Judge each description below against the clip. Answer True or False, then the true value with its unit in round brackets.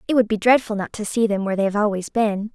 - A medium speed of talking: False (305 wpm)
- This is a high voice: True (215 Hz)